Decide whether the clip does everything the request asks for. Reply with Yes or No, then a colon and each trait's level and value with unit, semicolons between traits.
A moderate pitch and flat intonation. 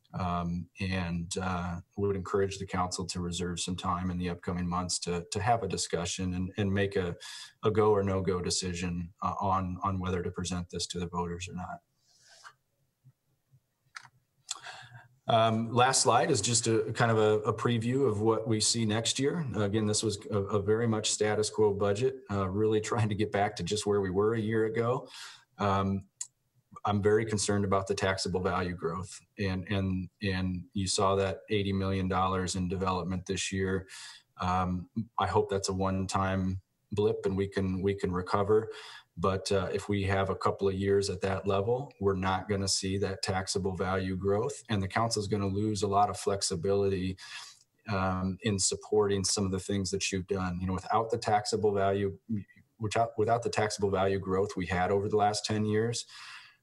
No: low, 100 Hz; narrow, 2.3 semitones